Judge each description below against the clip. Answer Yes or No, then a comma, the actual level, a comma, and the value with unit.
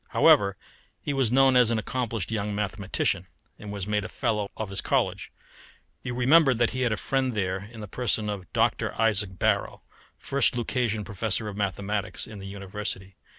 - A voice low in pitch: Yes, low, 105 Hz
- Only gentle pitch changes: No, average, 3.3 semitones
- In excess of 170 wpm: Yes, average, 180 wpm